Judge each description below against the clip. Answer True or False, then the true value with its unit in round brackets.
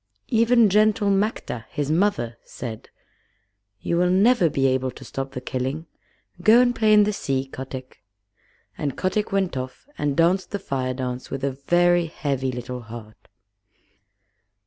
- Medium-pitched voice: True (145 Hz)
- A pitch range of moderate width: False (7.5 semitones)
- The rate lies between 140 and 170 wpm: True (150 wpm)